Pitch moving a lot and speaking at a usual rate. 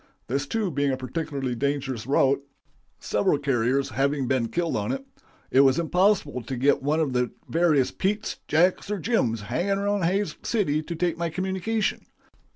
Yes: wide, 5.8 semitones; average, 165 wpm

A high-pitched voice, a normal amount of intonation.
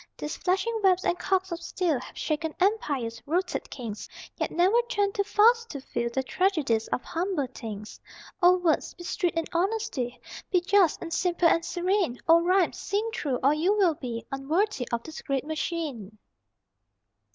No: very high, 335 Hz; wide, 5.9 semitones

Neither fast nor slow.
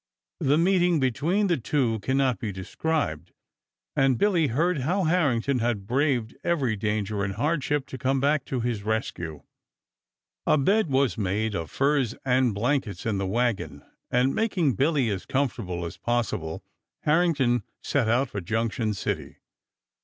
Yes: average, 150 wpm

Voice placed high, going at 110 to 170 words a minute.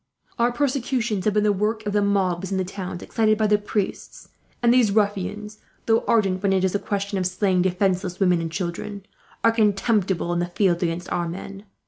No: high, 200 Hz; average, 200 wpm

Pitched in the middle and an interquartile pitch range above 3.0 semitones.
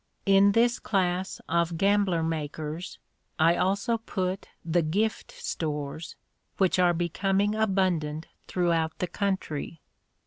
Yes: medium, 180 Hz; average, 3.4 semitones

